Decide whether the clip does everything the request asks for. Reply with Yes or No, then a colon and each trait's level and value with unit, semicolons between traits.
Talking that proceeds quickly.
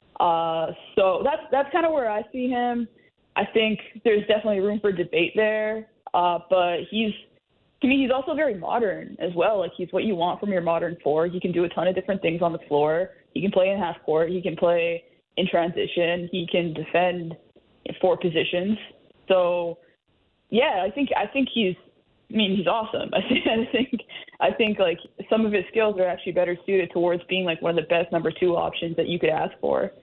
Yes: fast, 215 wpm